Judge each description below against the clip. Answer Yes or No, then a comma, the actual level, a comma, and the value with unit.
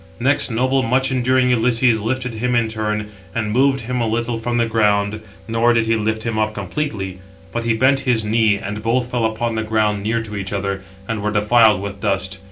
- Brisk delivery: Yes, fast, 210 wpm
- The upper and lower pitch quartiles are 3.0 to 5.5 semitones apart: No, narrow, 2.4 semitones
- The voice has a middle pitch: No, low, 115 Hz